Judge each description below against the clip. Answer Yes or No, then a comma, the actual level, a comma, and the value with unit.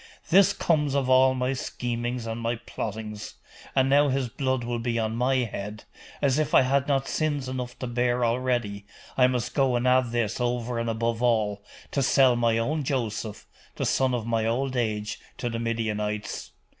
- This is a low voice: Yes, low, 120 Hz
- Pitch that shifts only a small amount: Yes, narrow, 2.3 semitones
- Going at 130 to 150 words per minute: No, average, 185 wpm